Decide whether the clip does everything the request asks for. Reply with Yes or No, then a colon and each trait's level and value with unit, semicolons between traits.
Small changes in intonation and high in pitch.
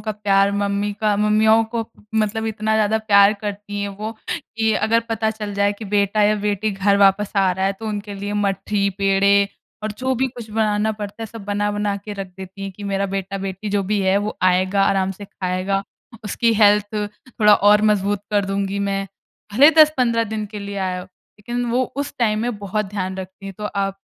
Yes: narrow, 1.5 semitones; high, 205 Hz